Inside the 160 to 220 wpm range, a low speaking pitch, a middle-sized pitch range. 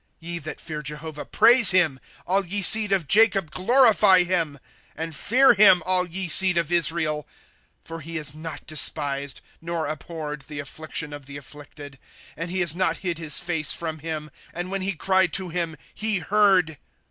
No: average, 180 wpm; medium, 165 Hz; average, 3.5 semitones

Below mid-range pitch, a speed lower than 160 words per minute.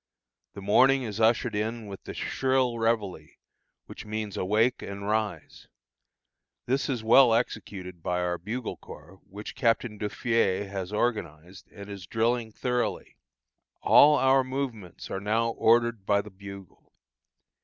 Yes: low, 110 Hz; slow, 135 wpm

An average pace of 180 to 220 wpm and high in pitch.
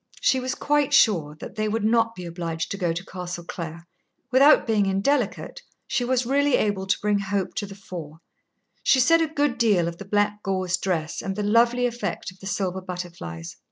Yes: average, 200 wpm; high, 200 Hz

